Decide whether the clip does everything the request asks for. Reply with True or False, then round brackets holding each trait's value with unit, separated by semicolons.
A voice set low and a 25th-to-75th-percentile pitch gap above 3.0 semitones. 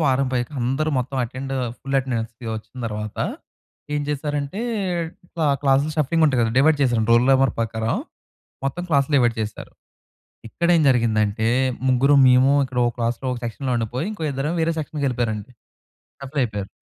True (130 Hz; 3.5 semitones)